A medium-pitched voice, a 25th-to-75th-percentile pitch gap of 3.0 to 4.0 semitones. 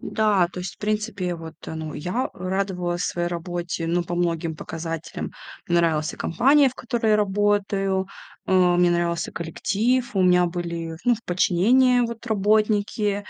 Yes: medium, 180 Hz; average, 3.6 semitones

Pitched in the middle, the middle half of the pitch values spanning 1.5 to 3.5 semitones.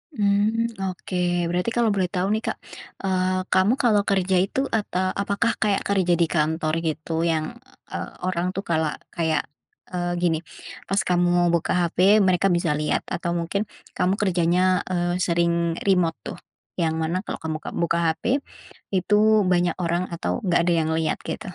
Yes: medium, 180 Hz; narrow, 2.5 semitones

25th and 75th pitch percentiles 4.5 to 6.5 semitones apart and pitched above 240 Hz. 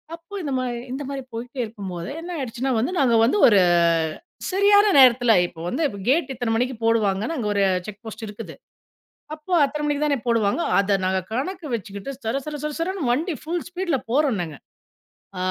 Yes: wide, 5.6 semitones; very high, 255 Hz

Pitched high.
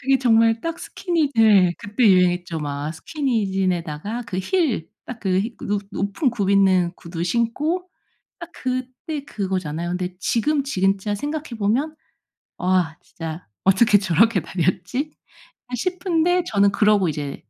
Yes: high, 205 Hz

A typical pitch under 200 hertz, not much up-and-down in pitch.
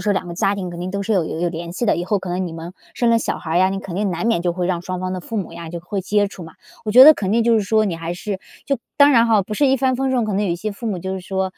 No: high, 190 Hz; average, 3.7 semitones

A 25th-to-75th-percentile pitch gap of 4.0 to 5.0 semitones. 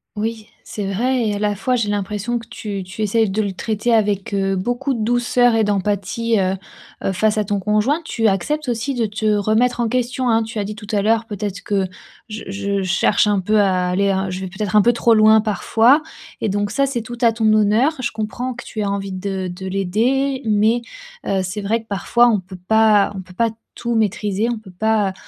No: average, 2.7 semitones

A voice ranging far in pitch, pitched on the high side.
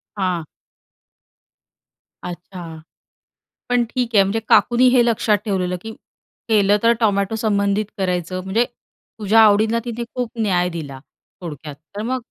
No: average, 3.8 semitones; high, 205 Hz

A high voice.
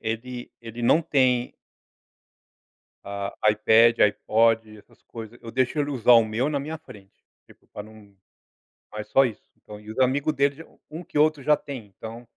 No: low, 120 Hz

